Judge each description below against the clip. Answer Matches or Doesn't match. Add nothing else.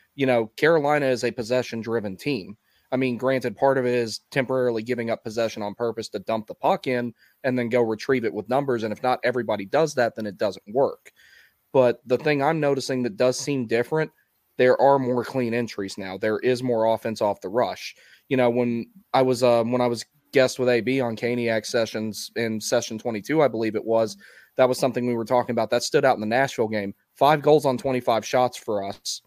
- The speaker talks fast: Matches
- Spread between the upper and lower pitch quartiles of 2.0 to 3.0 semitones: Matches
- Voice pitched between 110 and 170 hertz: Matches